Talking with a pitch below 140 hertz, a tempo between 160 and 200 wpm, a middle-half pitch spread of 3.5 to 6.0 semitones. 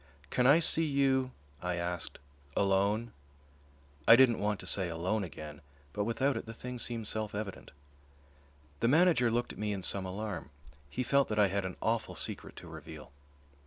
Yes: low, 110 Hz; average, 175 wpm; average, 4.5 semitones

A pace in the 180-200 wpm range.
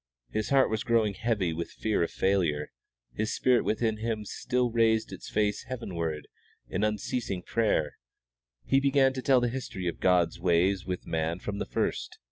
No: average, 170 wpm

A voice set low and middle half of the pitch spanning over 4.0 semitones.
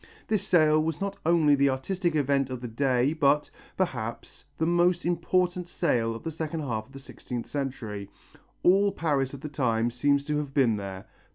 No: medium, 145 Hz; average, 5.2 semitones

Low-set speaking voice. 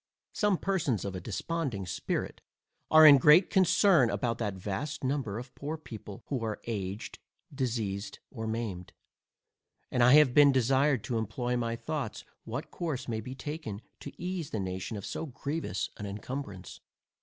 Yes: low, 125 Hz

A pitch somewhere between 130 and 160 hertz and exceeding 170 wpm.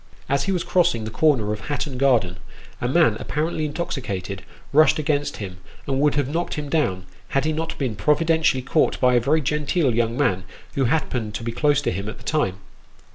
Yes: medium, 140 Hz; fast, 205 wpm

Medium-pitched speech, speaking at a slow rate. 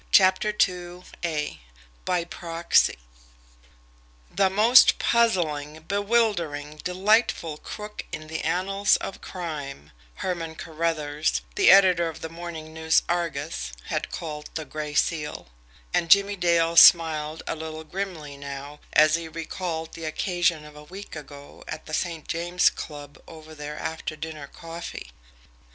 Yes: medium, 165 Hz; slow, 130 wpm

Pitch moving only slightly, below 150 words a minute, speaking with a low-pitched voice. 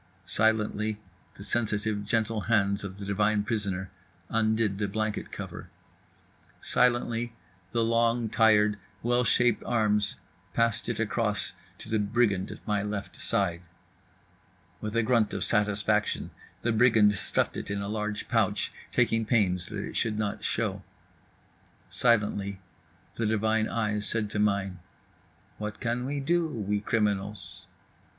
Yes: narrow, 1.9 semitones; slow, 135 wpm; low, 105 Hz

